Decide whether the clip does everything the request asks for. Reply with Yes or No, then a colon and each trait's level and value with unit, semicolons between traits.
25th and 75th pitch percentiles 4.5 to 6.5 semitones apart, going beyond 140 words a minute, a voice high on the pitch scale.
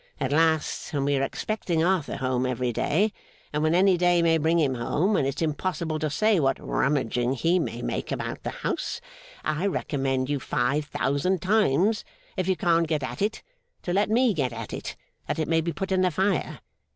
No: average, 5.1 semitones; average, 200 wpm; medium, 160 Hz